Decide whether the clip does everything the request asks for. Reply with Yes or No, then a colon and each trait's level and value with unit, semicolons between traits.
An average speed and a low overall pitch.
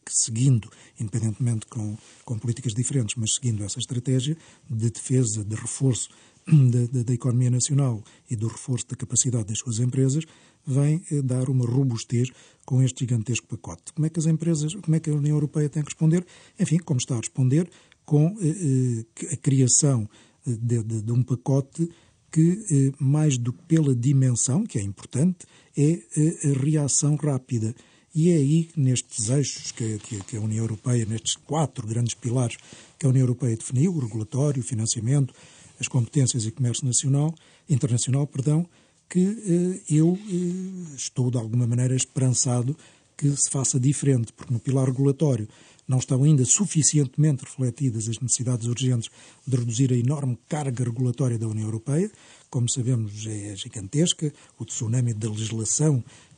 Yes: average, 155 wpm; low, 130 Hz